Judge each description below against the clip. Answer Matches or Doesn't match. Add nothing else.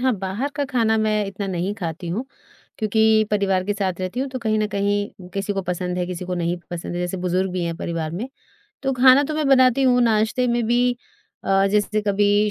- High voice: Matches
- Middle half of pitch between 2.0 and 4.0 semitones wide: Doesn't match